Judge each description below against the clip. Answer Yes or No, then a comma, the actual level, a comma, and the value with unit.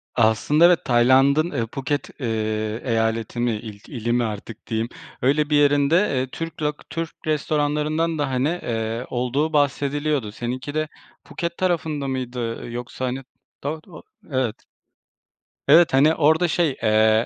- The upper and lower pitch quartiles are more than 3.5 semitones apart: Yes, average, 4.4 semitones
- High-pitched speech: No, low, 135 Hz